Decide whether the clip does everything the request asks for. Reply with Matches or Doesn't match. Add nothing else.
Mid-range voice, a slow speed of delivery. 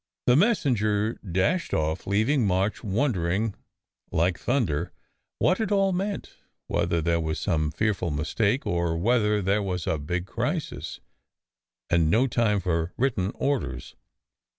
Doesn't match